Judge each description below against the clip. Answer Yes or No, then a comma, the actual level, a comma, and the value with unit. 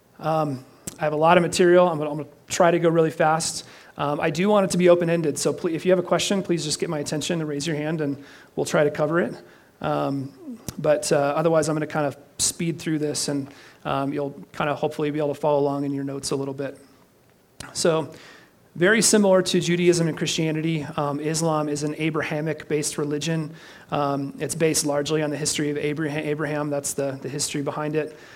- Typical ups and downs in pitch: No, narrow, 2.1 semitones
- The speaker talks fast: Yes, fast, 220 wpm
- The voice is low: No, medium, 150 Hz